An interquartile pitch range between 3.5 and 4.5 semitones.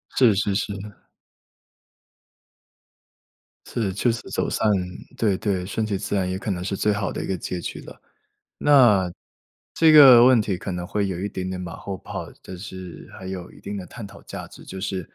No: average, 2.7 semitones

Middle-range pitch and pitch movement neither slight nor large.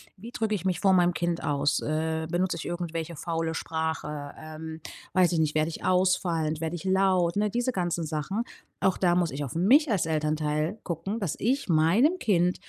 Yes: medium, 170 Hz; average, 3.1 semitones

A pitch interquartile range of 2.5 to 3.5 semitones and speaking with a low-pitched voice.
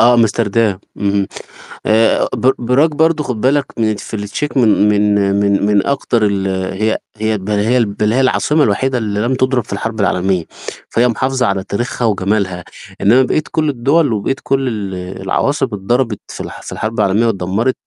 No: average, 4.1 semitones; low, 110 Hz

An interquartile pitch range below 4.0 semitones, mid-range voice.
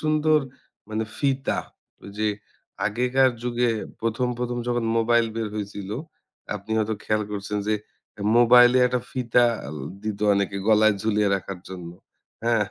No: average, 2.7 semitones; low, 115 Hz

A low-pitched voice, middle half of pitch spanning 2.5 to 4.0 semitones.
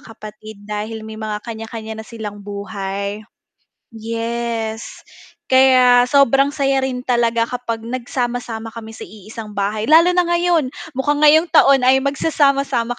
No: high, 230 Hz; average, 3.5 semitones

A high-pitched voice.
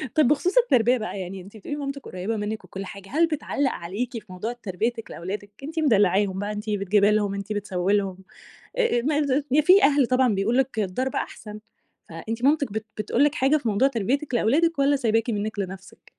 Yes: high, 225 Hz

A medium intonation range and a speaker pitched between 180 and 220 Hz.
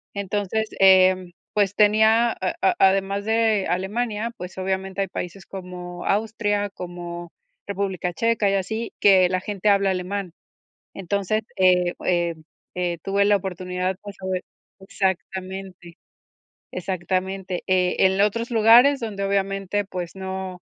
No: narrow, 1.9 semitones; high, 190 Hz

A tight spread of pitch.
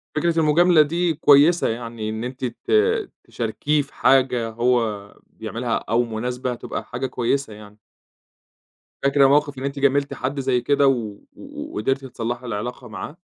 No: average, 3.4 semitones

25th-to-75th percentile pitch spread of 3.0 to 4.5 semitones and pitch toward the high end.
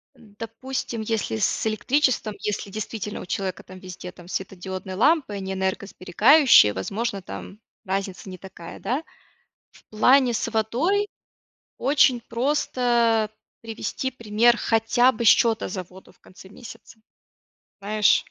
Yes: average, 4.1 semitones; high, 215 Hz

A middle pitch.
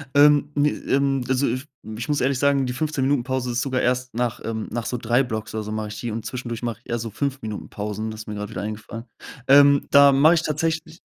No: low, 125 Hz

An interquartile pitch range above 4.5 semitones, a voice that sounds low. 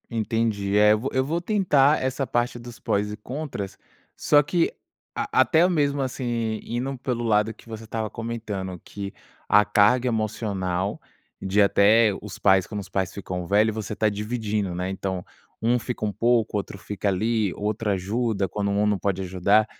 No: average, 3.1 semitones; low, 110 Hz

